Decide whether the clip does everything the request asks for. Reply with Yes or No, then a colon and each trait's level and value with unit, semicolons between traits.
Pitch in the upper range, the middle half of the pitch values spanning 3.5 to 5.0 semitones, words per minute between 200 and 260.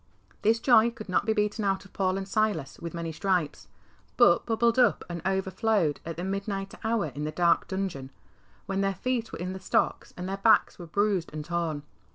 Yes: high, 195 Hz; average, 3.9 semitones; fast, 205 wpm